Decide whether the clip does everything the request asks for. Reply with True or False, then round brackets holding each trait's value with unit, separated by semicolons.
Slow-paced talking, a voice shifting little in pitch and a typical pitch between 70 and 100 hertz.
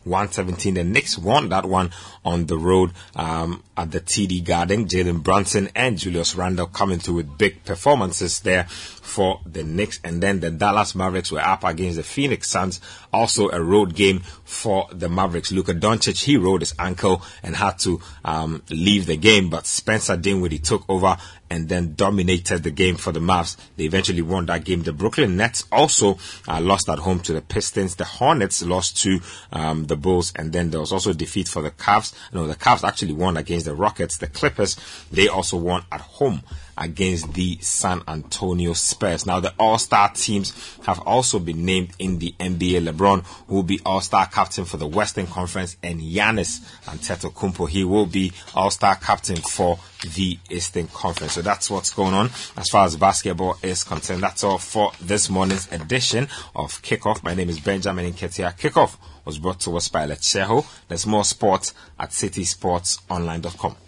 False (185 wpm; 2.3 semitones; 90 Hz)